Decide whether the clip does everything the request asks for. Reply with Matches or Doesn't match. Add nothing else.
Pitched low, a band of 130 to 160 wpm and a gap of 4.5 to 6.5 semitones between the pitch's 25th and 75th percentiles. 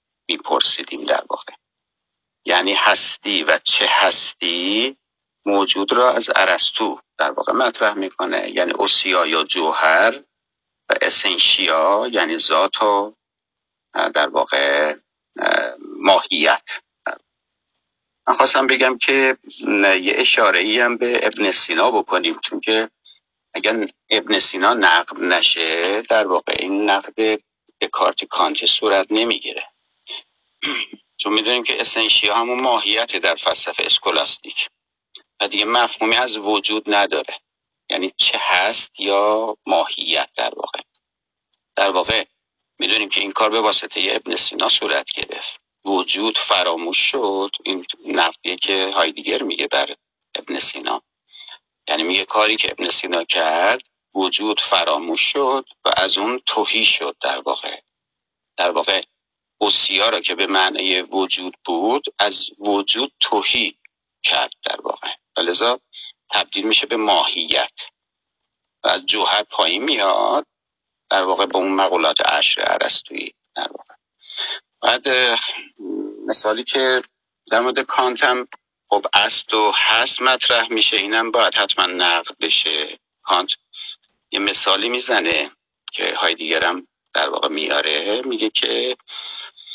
Doesn't match